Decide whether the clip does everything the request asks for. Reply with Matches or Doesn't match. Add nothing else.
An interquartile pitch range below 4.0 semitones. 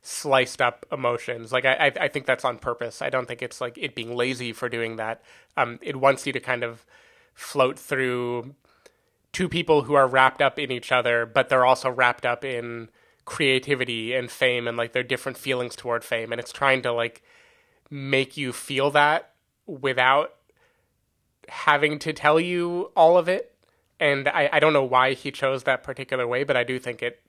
Matches